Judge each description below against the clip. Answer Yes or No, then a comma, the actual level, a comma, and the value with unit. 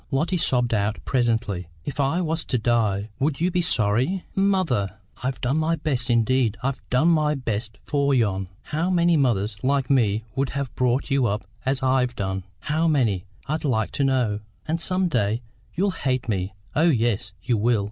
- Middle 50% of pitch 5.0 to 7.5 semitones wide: Yes, wide, 5.5 semitones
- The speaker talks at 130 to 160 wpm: No, average, 180 wpm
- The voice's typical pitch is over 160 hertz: No, low, 130 Hz